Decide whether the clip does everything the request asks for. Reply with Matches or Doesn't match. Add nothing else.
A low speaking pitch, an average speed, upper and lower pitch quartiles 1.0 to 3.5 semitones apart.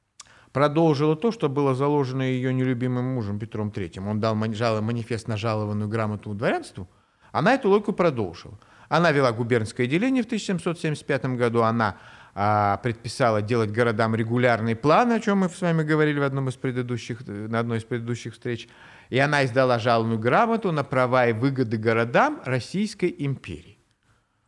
Doesn't match